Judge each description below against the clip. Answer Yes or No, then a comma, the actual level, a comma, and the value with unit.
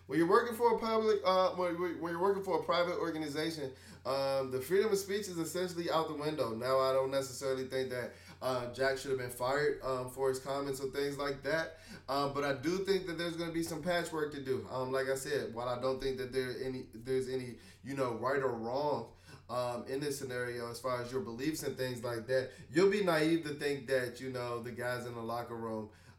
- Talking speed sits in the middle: No, fast, 240 wpm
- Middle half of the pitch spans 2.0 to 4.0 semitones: No, average, 4.7 semitones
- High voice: No, low, 135 Hz